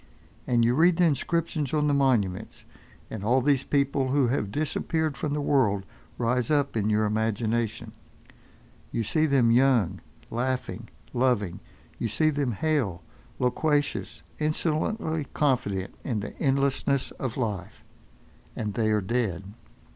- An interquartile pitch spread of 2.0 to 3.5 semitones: No, average, 5.0 semitones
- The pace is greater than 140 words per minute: No, slow, 135 wpm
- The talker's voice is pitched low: Yes, low, 125 Hz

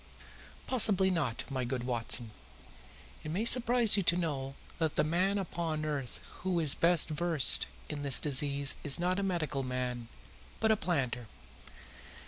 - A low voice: No, medium, 155 Hz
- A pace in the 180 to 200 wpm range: No, average, 150 wpm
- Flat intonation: No, average, 5.3 semitones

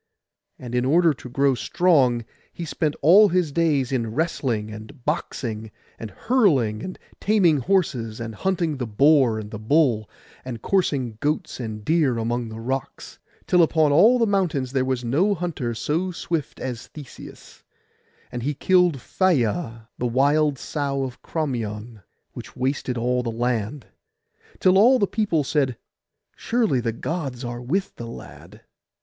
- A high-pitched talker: No, low, 135 Hz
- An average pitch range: No, wide, 5.9 semitones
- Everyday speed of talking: Yes, average, 155 wpm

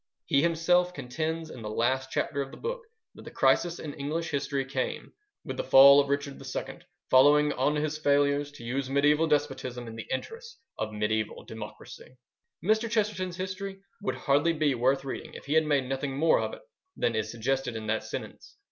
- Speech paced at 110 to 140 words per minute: No, average, 190 wpm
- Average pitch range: Yes, average, 3.9 semitones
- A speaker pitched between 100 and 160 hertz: Yes, medium, 140 Hz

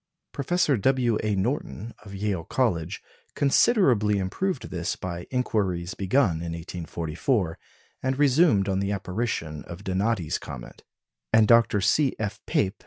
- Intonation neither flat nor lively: No, wide, 5.9 semitones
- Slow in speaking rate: Yes, slow, 125 wpm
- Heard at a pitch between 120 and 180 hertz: No, low, 100 Hz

